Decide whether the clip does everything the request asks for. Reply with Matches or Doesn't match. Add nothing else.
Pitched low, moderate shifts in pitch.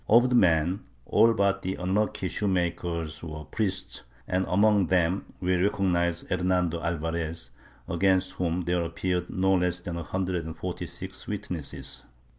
Doesn't match